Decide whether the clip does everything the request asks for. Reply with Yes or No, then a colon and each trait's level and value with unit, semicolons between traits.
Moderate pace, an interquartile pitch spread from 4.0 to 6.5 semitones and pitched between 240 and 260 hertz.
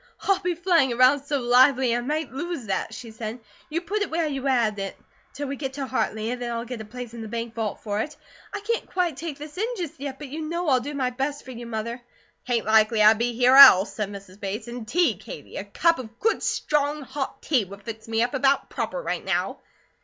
No: fast, 245 wpm; average, 4.6 semitones; very high, 255 Hz